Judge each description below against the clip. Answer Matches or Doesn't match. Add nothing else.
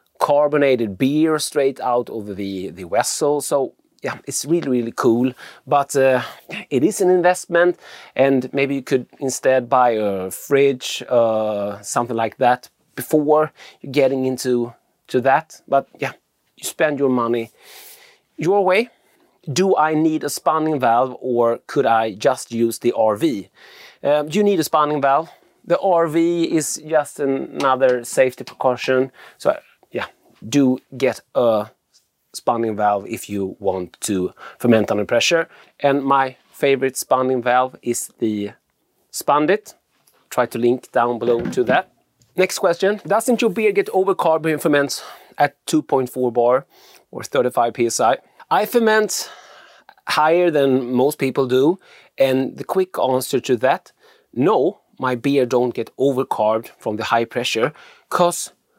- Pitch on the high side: Doesn't match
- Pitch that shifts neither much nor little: Matches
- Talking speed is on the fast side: Doesn't match